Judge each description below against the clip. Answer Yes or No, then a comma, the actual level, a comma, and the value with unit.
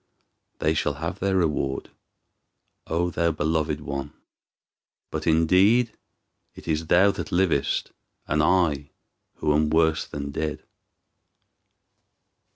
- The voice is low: Yes, very low, 80 Hz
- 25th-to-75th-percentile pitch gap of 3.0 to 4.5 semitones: No, narrow, 2.6 semitones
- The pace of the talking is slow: Yes, slow, 110 wpm